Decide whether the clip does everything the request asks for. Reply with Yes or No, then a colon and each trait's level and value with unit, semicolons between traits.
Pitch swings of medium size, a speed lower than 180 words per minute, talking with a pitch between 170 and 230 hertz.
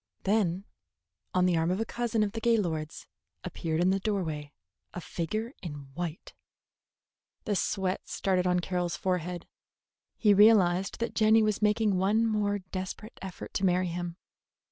Yes: average, 3.3 semitones; average, 150 wpm; high, 190 Hz